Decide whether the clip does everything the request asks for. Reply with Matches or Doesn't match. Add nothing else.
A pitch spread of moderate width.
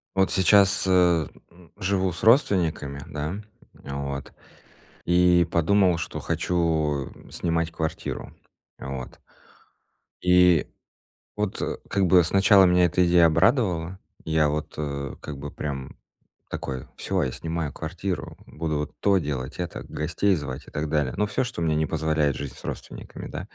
Matches